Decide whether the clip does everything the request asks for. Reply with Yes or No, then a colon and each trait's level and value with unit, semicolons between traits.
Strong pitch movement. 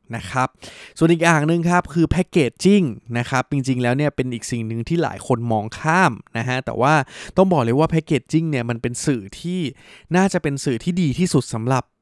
Yes: wide, 5.7 semitones